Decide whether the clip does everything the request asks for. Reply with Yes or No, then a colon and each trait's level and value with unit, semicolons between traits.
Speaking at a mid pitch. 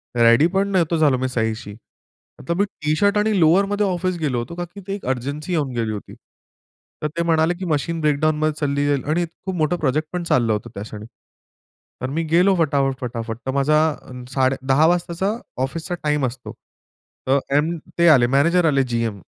Yes: medium, 155 Hz